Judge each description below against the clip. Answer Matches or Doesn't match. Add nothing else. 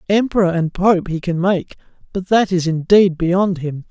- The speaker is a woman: Doesn't match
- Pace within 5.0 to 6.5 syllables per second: Doesn't match